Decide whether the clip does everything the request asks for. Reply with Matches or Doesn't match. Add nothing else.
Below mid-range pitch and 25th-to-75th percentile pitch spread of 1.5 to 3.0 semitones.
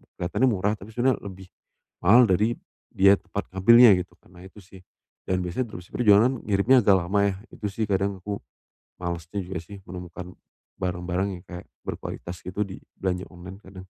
Matches